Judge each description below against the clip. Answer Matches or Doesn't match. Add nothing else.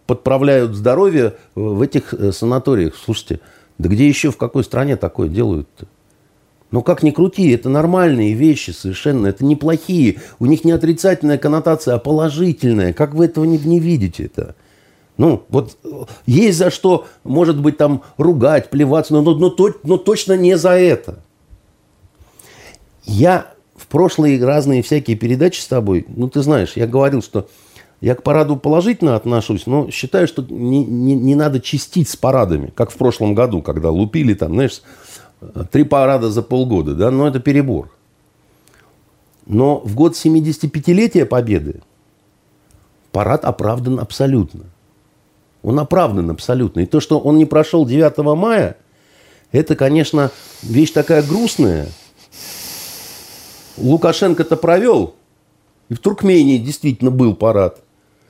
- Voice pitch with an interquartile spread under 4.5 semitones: Doesn't match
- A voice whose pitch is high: Doesn't match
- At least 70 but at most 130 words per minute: Doesn't match